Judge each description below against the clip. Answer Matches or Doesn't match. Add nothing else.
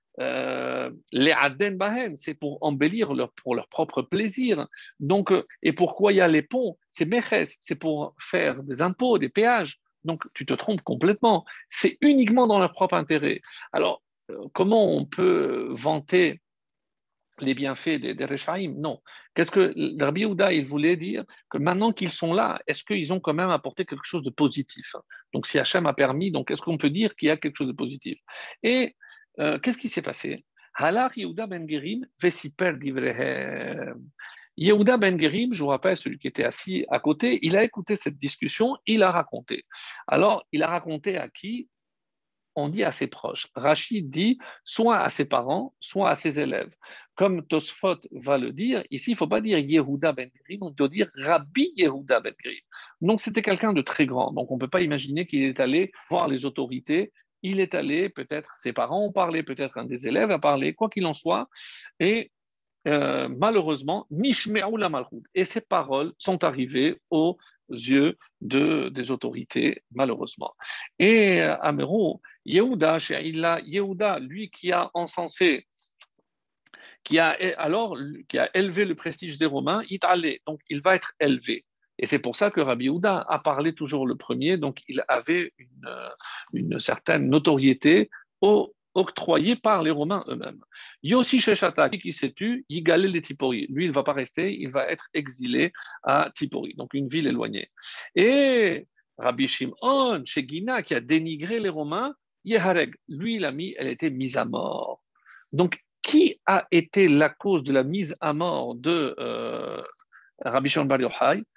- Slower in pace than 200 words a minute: Matches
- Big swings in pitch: Matches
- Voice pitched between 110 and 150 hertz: Doesn't match